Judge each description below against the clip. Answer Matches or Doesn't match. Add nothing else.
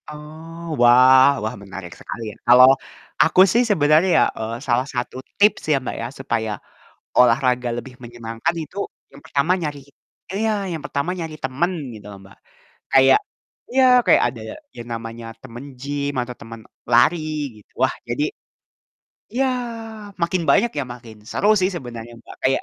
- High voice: Doesn't match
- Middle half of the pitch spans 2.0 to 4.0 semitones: Doesn't match